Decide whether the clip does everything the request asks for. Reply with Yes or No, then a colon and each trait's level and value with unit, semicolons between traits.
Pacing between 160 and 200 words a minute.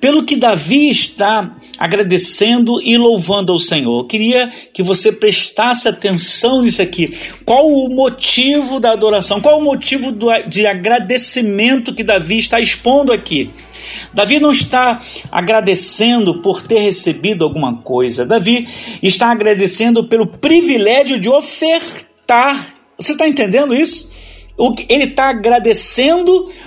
No: average, 130 wpm